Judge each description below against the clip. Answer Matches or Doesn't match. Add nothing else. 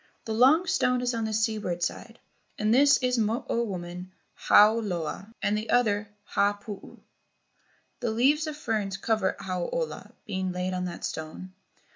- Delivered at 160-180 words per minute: Matches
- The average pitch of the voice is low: Doesn't match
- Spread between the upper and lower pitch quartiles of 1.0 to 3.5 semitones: Doesn't match